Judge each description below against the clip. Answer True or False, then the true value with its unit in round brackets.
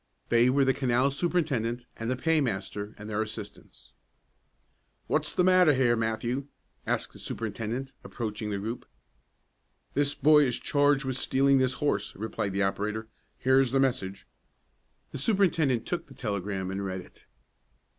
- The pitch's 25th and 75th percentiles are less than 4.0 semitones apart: False (4.5 semitones)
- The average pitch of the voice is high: False (120 Hz)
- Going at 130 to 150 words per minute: True (145 wpm)